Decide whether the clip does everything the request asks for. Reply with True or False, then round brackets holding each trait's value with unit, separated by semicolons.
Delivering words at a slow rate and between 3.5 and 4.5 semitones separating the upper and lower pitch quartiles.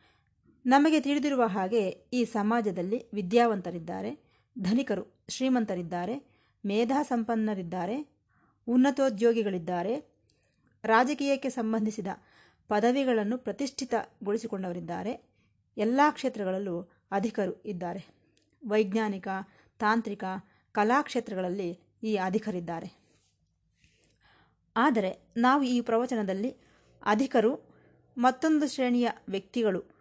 True (60 wpm; 4.2 semitones)